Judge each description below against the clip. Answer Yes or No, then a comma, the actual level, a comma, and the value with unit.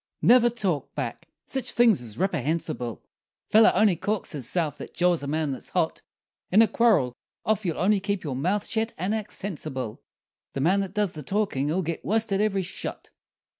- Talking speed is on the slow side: No, average, 180 wpm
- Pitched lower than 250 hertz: Yes, medium, 185 Hz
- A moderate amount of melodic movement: No, wide, 5.8 semitones